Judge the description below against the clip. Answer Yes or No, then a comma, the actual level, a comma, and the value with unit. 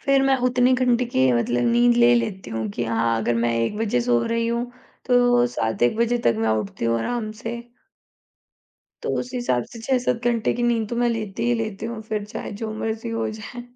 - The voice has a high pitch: Yes, high, 220 Hz